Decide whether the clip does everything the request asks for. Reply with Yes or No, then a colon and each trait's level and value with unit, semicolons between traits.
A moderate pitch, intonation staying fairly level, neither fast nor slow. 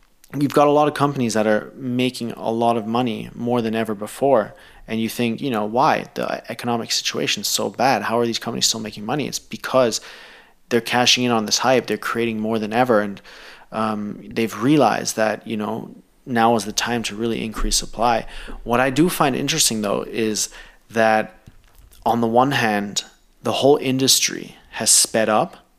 No: low, 115 Hz; narrow, 2.1 semitones; average, 190 wpm